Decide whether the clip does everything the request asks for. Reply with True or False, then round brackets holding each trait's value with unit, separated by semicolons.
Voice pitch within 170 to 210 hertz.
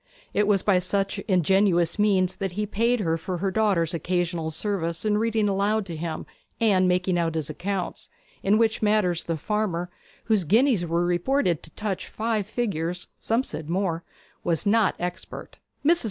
True (190 Hz)